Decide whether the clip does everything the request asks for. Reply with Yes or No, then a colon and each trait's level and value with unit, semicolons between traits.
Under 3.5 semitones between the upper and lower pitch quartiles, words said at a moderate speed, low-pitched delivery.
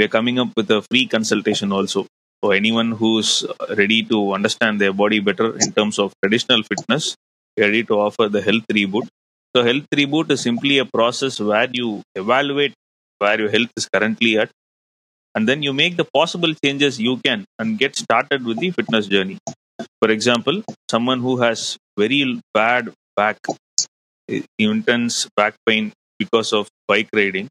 No: average, 4.4 semitones; average, 170 wpm; low, 115 Hz